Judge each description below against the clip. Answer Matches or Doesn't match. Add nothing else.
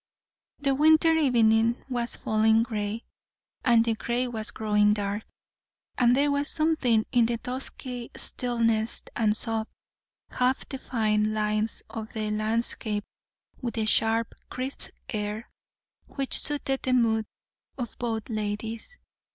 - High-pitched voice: Matches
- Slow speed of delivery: Matches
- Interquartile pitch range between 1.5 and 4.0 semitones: Matches